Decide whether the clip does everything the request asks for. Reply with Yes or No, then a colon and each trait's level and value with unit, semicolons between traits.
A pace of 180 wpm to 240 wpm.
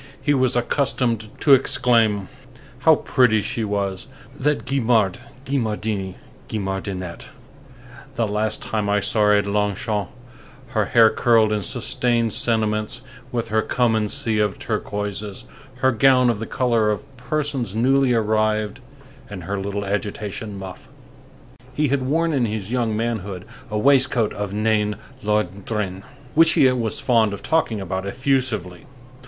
No: slow, 135 wpm